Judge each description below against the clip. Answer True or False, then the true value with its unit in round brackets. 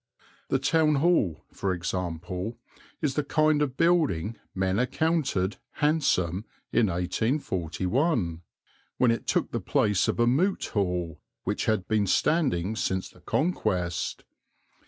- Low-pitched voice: True (110 Hz)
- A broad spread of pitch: True (8.5 semitones)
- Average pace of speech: False (125 wpm)